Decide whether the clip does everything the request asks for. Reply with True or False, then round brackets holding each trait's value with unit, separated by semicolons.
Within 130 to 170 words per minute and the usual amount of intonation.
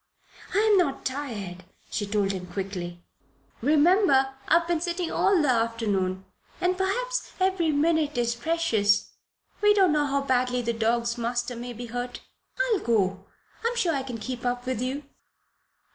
False (160 wpm; 6.7 semitones)